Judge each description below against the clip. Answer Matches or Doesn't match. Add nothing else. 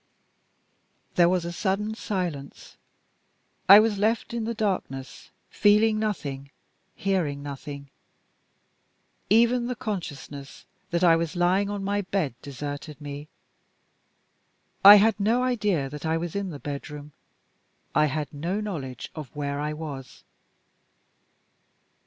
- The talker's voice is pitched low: Doesn't match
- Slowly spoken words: Matches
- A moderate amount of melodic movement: Doesn't match